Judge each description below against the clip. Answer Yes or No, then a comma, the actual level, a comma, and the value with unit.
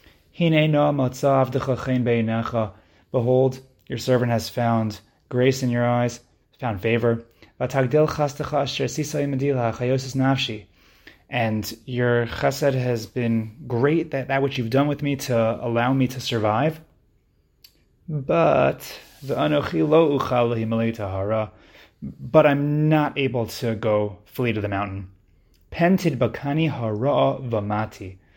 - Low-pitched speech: Yes, low, 120 Hz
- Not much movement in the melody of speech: No, average, 3.7 semitones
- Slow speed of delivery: Yes, slow, 90 wpm